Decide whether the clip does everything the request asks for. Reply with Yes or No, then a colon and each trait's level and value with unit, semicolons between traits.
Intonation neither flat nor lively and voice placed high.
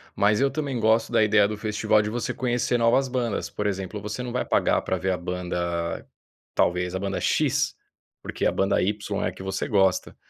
No: average, 3.5 semitones; low, 105 Hz